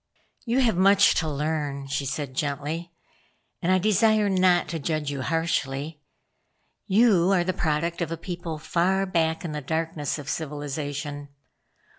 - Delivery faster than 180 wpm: No, average, 150 wpm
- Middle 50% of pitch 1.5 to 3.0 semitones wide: No, average, 3.8 semitones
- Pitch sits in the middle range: Yes, medium, 160 Hz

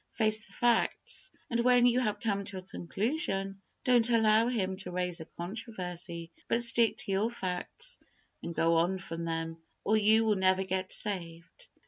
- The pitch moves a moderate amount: Yes, average, 4.2 semitones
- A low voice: No, high, 200 Hz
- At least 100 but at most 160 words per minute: No, average, 170 wpm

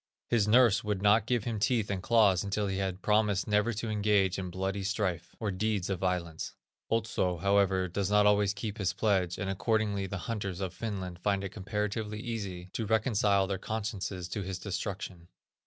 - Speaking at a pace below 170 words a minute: No, average, 185 wpm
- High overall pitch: No, low, 100 Hz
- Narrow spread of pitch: Yes, narrow, 2.2 semitones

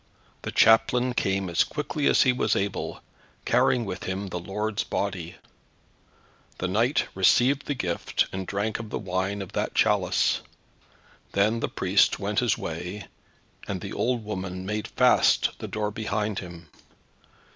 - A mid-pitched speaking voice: No, low, 100 Hz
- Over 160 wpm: No, average, 150 wpm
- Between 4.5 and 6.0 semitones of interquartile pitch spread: No, average, 3.1 semitones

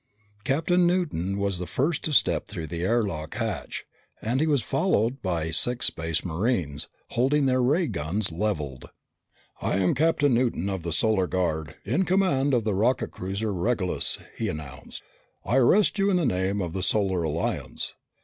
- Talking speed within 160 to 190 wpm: Yes, average, 170 wpm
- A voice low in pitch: Yes, low, 105 Hz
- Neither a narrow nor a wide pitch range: No, wide, 7.5 semitones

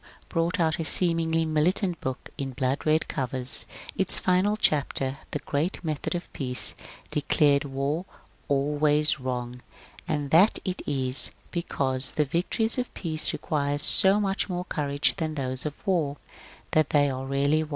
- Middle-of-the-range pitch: Yes, medium, 150 Hz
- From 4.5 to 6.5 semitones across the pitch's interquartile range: No, average, 3.6 semitones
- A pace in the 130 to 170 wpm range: Yes, average, 160 wpm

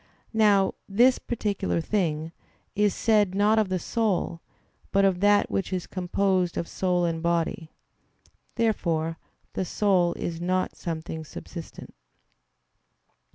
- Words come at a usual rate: No, slow, 120 wpm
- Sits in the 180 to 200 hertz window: Yes, medium, 185 Hz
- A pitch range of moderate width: Yes, average, 3.3 semitones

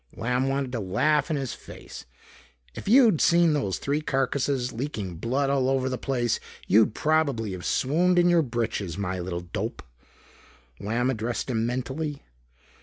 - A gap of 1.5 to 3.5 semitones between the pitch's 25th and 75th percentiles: No, average, 4.7 semitones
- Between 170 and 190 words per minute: No, average, 155 wpm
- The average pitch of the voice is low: Yes, low, 130 Hz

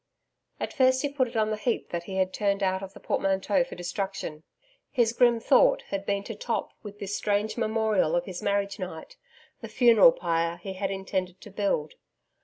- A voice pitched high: Yes, high, 200 Hz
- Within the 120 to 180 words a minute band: No, average, 200 wpm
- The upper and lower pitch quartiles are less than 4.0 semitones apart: Yes, average, 3.2 semitones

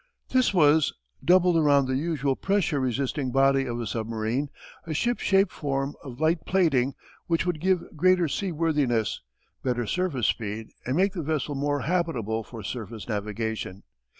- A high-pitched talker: No, medium, 140 Hz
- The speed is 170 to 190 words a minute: No, average, 150 wpm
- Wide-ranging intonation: Yes, wide, 5.8 semitones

